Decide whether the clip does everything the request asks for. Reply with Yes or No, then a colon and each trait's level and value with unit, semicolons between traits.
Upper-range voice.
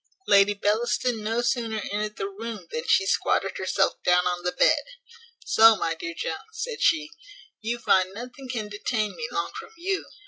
Yes: high, 215 Hz